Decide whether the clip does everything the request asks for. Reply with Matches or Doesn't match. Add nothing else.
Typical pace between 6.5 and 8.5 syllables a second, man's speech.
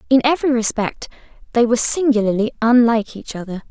Doesn't match